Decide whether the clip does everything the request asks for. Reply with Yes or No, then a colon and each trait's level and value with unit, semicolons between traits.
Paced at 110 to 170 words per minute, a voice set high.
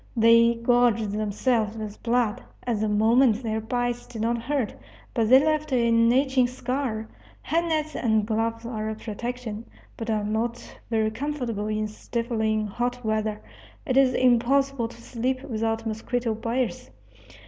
Yes: average, 150 wpm; high, 230 Hz